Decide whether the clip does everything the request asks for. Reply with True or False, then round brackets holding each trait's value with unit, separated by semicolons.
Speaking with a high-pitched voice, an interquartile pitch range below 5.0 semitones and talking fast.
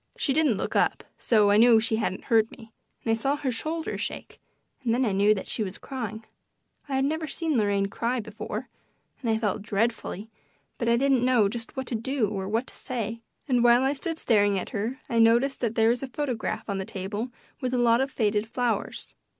True (230 Hz; 3.2 semitones; 220 wpm)